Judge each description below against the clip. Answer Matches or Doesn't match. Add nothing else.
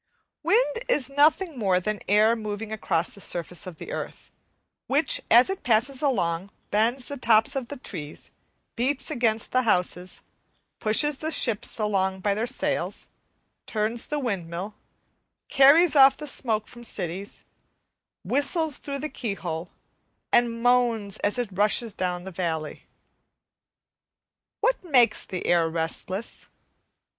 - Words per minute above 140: Doesn't match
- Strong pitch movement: Matches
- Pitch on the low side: Doesn't match